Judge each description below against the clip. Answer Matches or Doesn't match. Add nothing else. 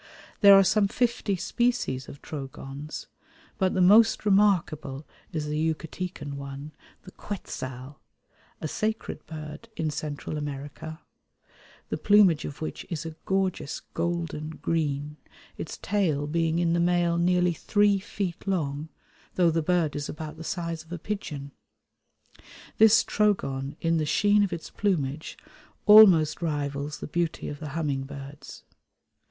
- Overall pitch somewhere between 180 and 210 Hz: Doesn't match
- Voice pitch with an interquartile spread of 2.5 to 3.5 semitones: Doesn't match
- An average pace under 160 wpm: Matches